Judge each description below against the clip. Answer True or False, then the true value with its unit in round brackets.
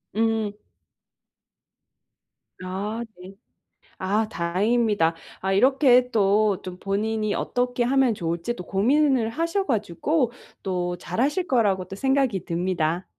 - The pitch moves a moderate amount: True (4.8 semitones)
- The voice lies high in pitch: True (215 Hz)